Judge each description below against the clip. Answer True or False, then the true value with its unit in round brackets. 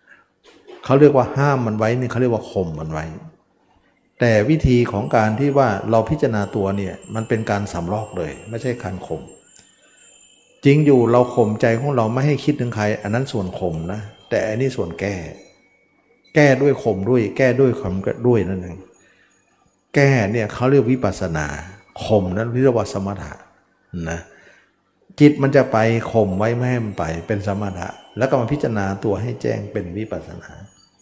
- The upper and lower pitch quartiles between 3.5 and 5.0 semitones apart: True (4.5 semitones)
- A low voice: True (110 Hz)